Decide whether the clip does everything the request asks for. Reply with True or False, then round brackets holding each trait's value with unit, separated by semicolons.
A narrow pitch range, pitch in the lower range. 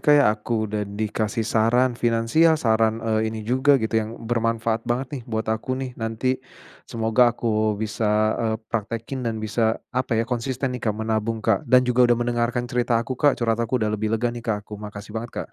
True (1.9 semitones; 115 Hz)